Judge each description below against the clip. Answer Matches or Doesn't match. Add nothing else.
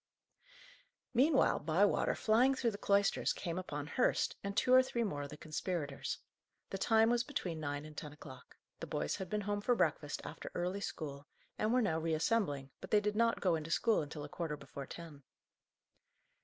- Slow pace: Doesn't match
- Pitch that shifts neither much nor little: Doesn't match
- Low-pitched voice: Doesn't match